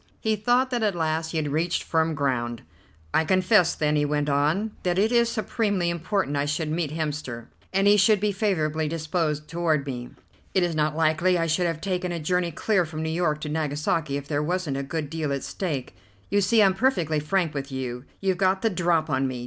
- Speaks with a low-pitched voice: No, medium, 160 Hz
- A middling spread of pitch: Yes, average, 3.8 semitones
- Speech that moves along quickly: Yes, fast, 215 wpm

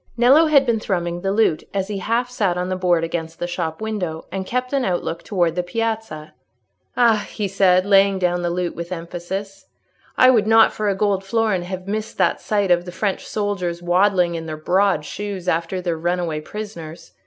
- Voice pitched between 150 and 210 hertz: Yes, medium, 185 Hz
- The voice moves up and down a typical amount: Yes, average, 3.3 semitones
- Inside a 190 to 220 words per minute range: Yes, average, 200 wpm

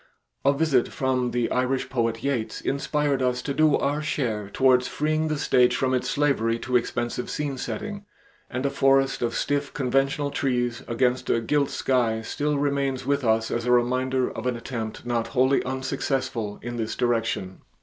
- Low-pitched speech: Yes, low, 130 Hz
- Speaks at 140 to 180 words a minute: Yes, average, 170 wpm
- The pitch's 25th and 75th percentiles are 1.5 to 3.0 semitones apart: Yes, narrow, 2.6 semitones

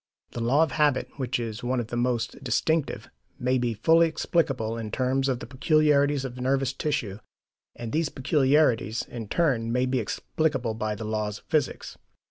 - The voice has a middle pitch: No, low, 130 Hz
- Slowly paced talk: No, average, 175 wpm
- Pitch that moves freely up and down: No, average, 3.9 semitones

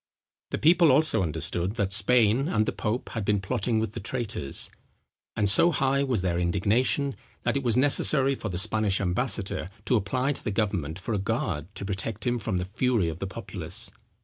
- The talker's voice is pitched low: Yes, low, 105 Hz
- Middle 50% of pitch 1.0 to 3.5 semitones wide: No, average, 4.9 semitones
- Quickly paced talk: No, average, 195 wpm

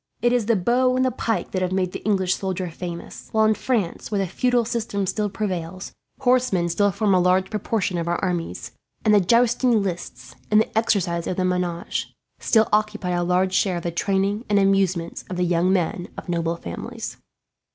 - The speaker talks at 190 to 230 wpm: Yes, average, 200 wpm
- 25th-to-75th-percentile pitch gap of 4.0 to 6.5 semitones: No, average, 3.4 semitones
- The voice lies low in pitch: No, high, 190 Hz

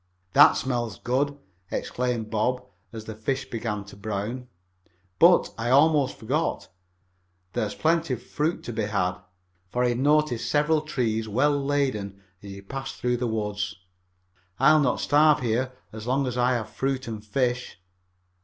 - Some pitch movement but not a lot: Yes, average, 4.0 semitones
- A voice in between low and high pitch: No, low, 125 Hz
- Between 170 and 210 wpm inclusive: No, average, 155 wpm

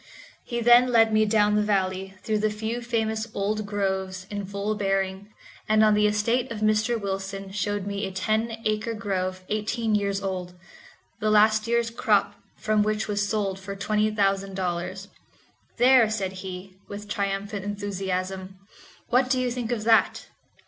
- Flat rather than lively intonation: Yes, narrow, 2.0 semitones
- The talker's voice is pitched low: No, high, 210 Hz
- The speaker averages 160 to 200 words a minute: Yes, average, 165 wpm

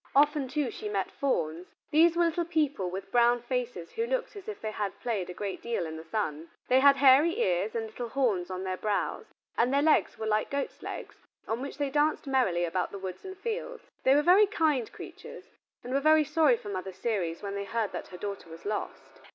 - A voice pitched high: Yes, high, 240 Hz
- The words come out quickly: Yes, fast, 225 wpm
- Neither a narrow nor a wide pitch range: No, wide, 7.3 semitones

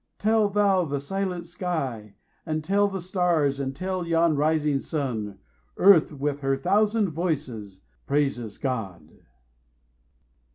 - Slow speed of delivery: Yes, slow, 120 wpm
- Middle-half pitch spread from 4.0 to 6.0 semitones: Yes, average, 5.2 semitones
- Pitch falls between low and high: Yes, medium, 155 Hz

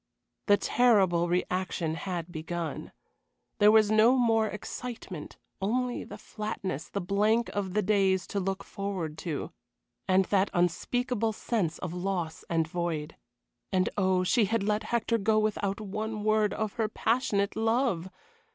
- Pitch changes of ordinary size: Yes, average, 3.4 semitones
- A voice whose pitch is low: No, high, 200 Hz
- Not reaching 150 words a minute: Yes, average, 140 wpm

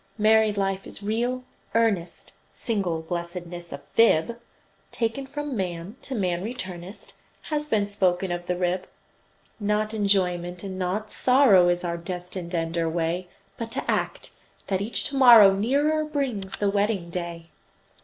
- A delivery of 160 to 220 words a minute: No, average, 145 wpm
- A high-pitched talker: Yes, high, 195 Hz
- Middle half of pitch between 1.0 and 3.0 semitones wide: No, average, 4.2 semitones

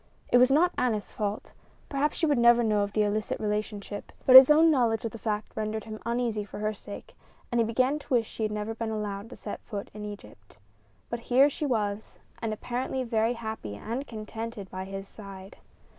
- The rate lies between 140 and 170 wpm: No, fast, 205 wpm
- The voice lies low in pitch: No, high, 220 Hz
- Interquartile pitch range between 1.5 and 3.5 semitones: Yes, average, 2.7 semitones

